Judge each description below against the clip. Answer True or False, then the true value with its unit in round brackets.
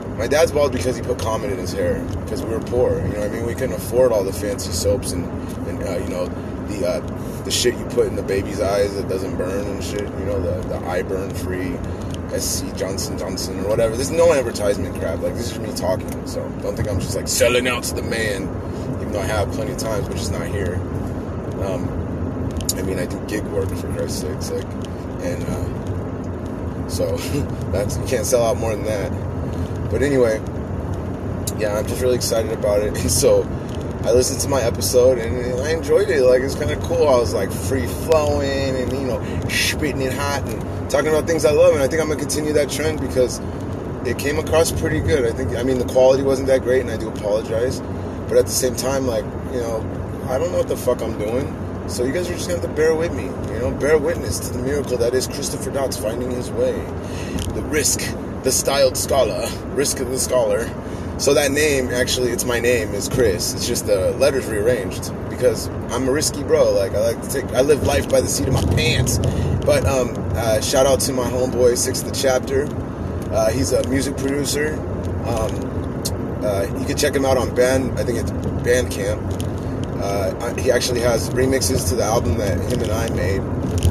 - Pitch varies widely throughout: True (5.7 semitones)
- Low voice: True (105 Hz)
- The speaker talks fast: True (215 wpm)